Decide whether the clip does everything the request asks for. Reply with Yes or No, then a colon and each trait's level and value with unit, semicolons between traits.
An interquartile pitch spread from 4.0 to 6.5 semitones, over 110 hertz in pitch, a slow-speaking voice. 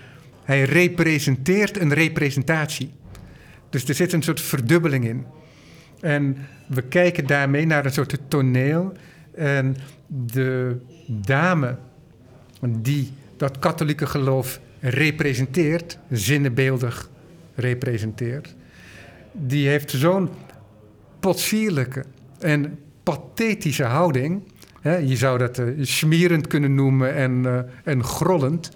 No: average, 3.6 semitones; medium, 140 Hz; slow, 90 wpm